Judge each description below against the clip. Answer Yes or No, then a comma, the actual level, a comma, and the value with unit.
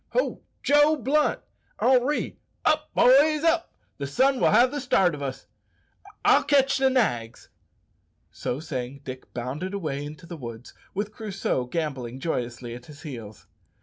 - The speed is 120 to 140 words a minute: No, average, 150 wpm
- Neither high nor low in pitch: Yes, medium, 165 Hz